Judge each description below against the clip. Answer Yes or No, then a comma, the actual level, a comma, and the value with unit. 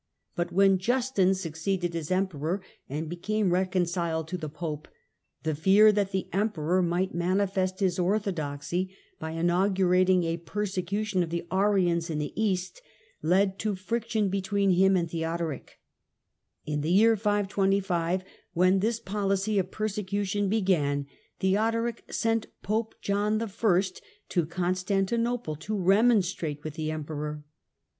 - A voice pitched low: No, medium, 185 Hz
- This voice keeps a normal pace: No, slow, 130 wpm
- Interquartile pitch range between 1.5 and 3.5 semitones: Yes, average, 3.1 semitones